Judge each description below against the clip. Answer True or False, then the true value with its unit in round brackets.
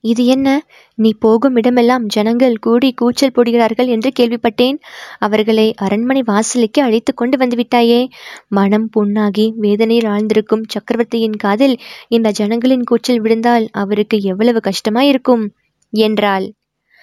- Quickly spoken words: False (110 wpm)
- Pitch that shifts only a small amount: True (2.2 semitones)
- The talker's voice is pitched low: False (230 Hz)